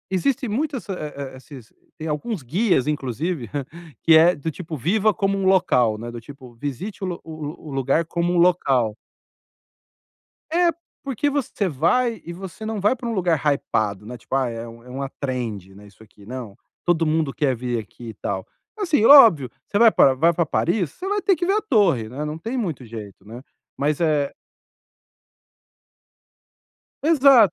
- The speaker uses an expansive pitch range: Yes, wide, 8.4 semitones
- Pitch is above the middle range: No, medium, 155 Hz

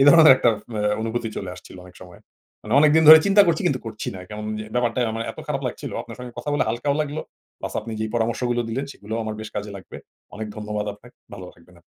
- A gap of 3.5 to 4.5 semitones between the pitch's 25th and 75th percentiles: Yes, average, 4.0 semitones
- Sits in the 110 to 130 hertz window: Yes, low, 115 Hz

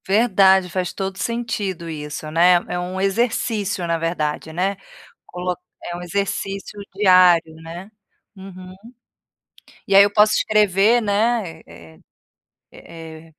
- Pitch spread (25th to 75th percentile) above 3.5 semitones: No, average, 3.2 semitones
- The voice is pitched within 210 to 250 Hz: No, medium, 185 Hz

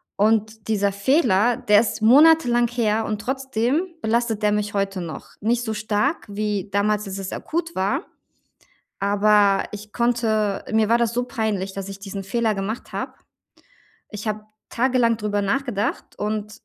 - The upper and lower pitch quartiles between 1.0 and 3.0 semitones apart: Yes, average, 2.7 semitones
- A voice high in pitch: Yes, high, 215 Hz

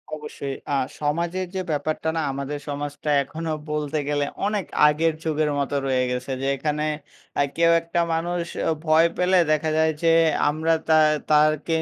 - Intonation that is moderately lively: No, narrow, 2.1 semitones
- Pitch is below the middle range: No, medium, 155 Hz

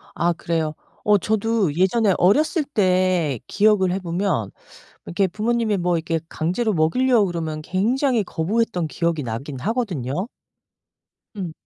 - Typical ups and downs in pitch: Yes, average, 4.9 semitones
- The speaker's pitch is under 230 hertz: Yes, medium, 185 Hz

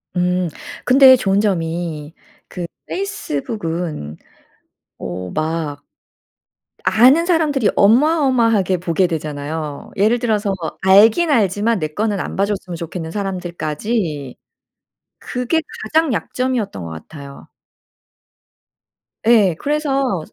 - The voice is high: Yes, high, 195 Hz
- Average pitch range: No, wide, 6.8 semitones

